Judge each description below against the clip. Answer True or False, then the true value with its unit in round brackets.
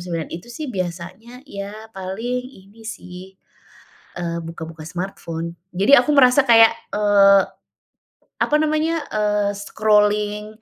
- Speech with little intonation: False (4.5 semitones)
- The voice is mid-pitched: False (205 Hz)